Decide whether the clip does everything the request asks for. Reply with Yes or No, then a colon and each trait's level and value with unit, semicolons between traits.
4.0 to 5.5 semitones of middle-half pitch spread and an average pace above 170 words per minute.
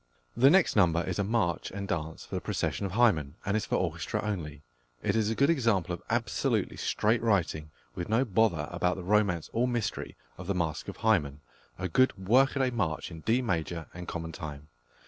Yes: average, 5.2 semitones; average, 200 wpm